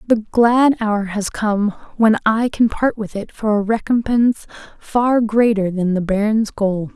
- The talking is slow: No, average, 175 wpm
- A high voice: Yes, high, 215 Hz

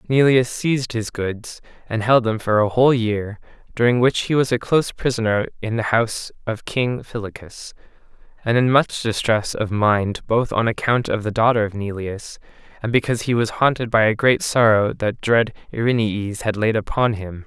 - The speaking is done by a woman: No, male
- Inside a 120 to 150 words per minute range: No, average, 185 wpm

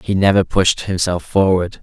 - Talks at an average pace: Yes, average, 165 wpm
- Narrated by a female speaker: No, male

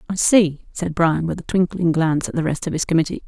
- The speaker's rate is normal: No, fast, 255 wpm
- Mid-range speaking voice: Yes, medium, 170 Hz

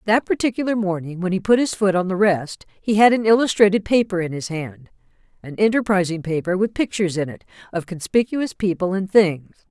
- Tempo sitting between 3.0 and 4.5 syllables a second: No, 5.6 syllables/s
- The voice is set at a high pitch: Yes, high, 195 Hz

